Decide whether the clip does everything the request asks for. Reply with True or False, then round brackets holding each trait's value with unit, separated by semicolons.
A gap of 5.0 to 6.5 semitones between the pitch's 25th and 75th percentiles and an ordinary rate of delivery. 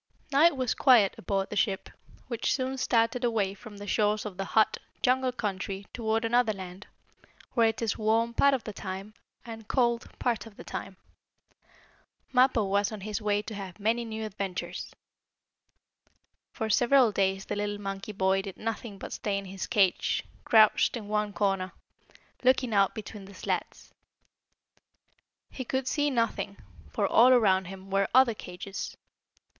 False (3.2 semitones; 160 wpm)